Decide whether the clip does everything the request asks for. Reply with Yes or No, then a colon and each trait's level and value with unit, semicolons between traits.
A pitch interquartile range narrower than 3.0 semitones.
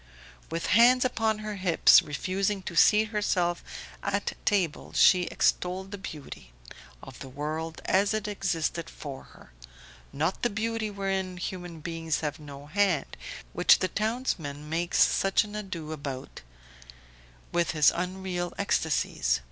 No: average, 4.4 semitones